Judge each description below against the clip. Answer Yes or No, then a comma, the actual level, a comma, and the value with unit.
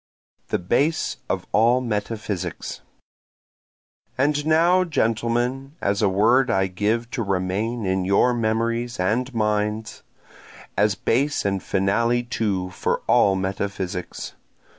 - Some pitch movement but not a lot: Yes, average, 3.7 semitones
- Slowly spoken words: Yes, slow, 110 wpm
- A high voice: No, low, 110 Hz